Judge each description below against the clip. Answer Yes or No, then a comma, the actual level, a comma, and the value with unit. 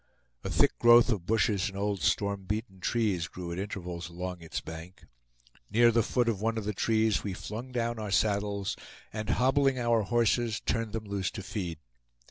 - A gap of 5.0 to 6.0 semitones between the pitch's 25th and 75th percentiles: No, average, 3.3 semitones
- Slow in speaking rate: No, average, 185 wpm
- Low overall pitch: Yes, low, 105 Hz